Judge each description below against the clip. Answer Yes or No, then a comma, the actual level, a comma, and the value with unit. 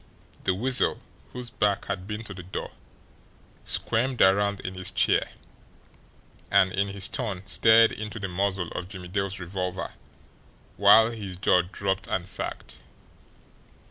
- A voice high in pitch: No, low, 100 Hz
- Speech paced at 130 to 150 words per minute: Yes, average, 140 wpm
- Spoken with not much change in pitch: Yes, narrow, 2.3 semitones